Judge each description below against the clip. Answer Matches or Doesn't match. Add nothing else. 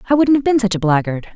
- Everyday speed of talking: Doesn't match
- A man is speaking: Doesn't match